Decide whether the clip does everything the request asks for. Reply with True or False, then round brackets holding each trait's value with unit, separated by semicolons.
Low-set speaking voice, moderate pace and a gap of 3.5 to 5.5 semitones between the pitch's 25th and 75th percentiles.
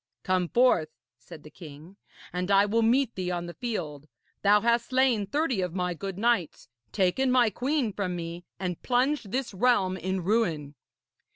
False (195 Hz; 170 wpm; 5.2 semitones)